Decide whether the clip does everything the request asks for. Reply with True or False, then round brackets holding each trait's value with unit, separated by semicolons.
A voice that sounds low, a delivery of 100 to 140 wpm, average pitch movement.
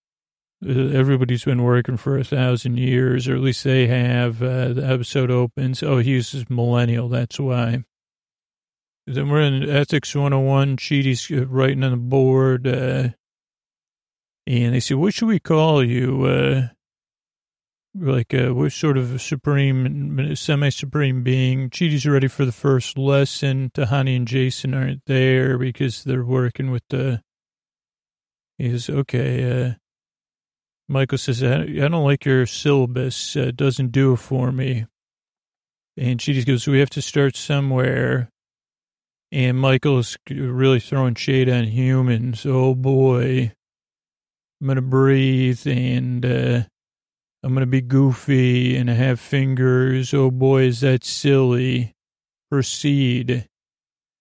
False (130 Hz; 135 wpm; 1.5 semitones)